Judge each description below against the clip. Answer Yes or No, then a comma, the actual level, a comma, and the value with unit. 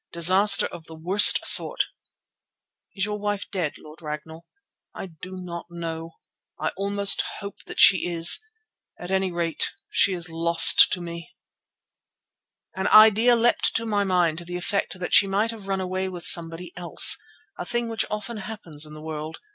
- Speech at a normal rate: Yes, average, 170 wpm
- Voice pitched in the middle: Yes, medium, 180 Hz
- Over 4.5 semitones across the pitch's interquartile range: No, average, 3.2 semitones